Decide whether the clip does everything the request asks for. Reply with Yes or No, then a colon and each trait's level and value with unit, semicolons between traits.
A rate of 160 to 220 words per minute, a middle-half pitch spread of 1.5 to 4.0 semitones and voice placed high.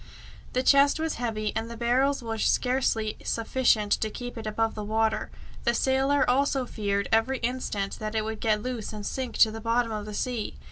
Yes: average, 190 wpm; average, 2.8 semitones; high, 230 Hz